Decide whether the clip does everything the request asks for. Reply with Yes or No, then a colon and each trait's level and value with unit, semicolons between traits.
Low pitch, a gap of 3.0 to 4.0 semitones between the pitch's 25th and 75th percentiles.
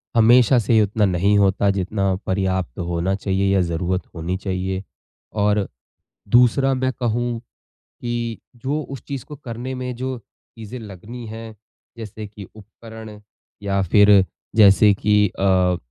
Yes: low, 105 Hz; average, 3.6 semitones